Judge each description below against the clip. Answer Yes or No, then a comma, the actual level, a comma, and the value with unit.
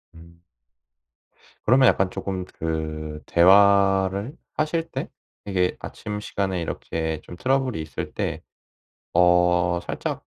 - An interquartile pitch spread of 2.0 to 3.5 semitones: Yes, average, 3.2 semitones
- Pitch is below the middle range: Yes, very low, 90 Hz